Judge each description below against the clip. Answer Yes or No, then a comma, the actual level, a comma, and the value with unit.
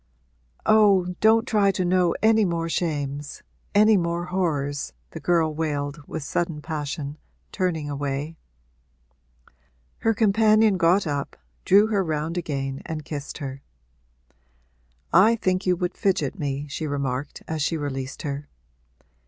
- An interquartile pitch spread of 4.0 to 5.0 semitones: Yes, average, 4.6 semitones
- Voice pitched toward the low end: No, medium, 165 Hz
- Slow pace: Yes, slow, 130 wpm